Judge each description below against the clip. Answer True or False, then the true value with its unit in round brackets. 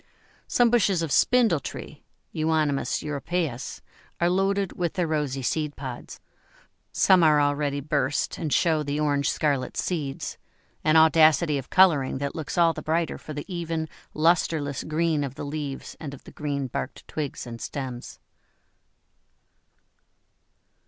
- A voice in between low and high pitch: True (150 Hz)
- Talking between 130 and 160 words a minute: True (140 wpm)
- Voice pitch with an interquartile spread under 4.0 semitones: True (2.8 semitones)